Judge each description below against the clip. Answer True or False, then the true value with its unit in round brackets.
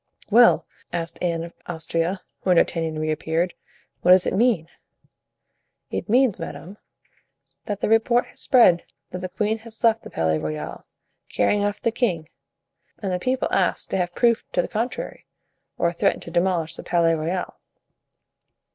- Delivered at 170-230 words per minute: False (155 wpm)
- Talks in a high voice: False (180 Hz)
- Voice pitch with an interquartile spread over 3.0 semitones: True (4.9 semitones)